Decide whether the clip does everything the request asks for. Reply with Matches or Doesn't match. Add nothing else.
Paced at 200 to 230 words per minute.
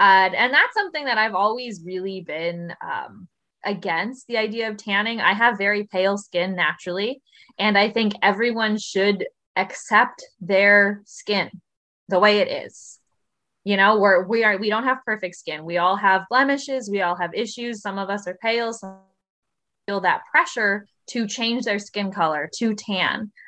Doesn't match